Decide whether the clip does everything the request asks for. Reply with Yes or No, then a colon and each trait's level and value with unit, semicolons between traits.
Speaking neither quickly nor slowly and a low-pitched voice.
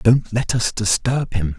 Yes: average, 190 wpm; low, 115 Hz